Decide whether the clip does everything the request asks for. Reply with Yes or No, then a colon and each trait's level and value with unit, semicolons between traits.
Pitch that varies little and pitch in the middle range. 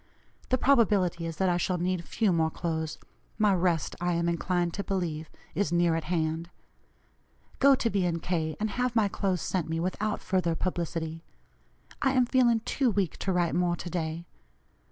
No: average, 3.5 semitones; medium, 175 Hz